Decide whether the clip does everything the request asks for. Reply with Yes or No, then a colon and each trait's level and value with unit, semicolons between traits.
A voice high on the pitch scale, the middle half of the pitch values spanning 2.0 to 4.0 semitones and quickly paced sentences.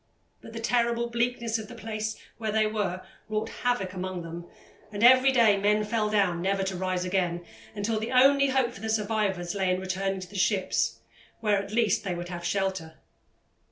No: high, 205 Hz; average, 3.5 semitones; average, 195 wpm